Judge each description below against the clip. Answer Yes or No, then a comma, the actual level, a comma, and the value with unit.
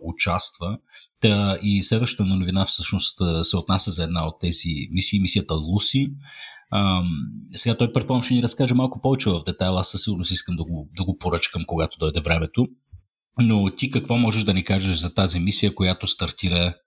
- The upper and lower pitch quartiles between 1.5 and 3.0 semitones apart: No, average, 4.0 semitones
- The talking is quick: Yes, fast, 170 wpm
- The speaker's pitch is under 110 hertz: Yes, very low, 95 Hz